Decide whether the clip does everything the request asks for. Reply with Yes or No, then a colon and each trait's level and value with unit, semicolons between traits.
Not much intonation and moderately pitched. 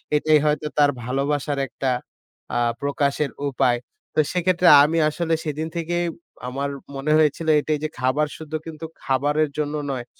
Yes: narrow, 2.0 semitones; medium, 150 Hz